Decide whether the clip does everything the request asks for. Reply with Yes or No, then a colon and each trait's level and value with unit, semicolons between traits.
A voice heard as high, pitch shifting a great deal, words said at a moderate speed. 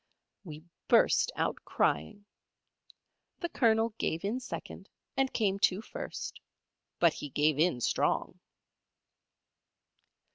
No: high, 195 Hz; wide, 6.5 semitones; slow, 105 wpm